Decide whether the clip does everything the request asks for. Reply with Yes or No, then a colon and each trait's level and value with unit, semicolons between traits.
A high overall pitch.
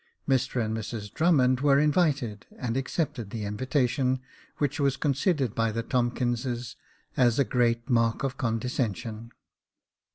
No: low, 125 Hz